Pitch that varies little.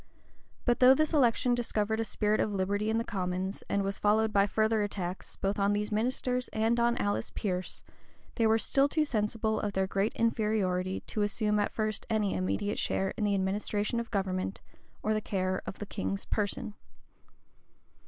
Yes: narrow, 2.3 semitones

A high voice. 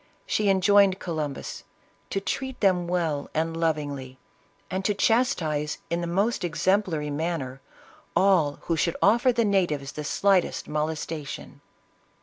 No: medium, 170 Hz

